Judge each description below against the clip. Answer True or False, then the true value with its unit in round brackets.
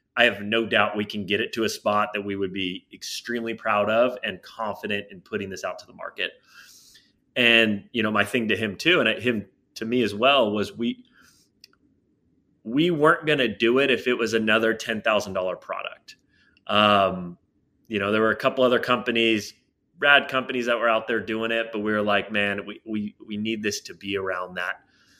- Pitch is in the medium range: False (110 Hz)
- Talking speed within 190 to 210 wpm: True (205 wpm)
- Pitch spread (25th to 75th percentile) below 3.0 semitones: True (2.6 semitones)